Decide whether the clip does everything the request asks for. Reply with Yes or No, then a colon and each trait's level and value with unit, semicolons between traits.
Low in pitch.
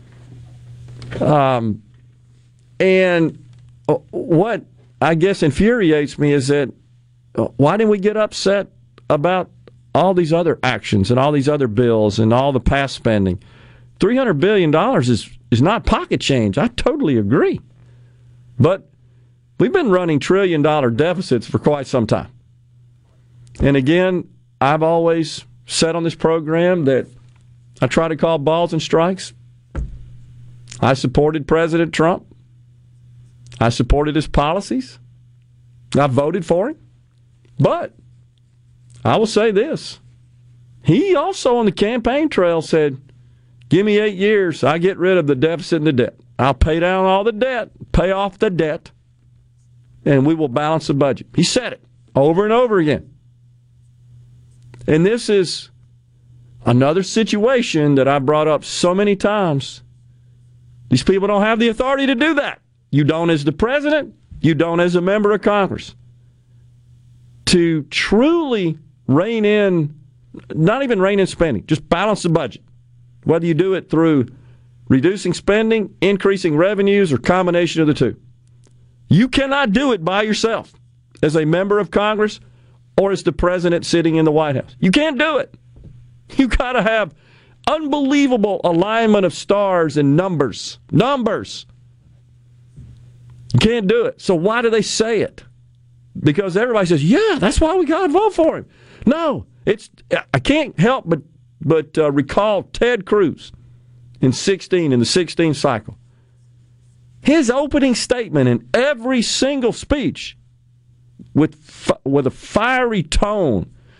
No: medium, 145 Hz